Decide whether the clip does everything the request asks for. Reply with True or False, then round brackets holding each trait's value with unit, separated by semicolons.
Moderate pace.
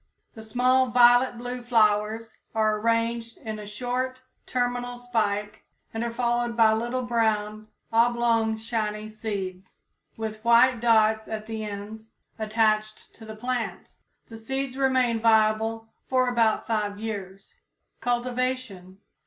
False (125 wpm)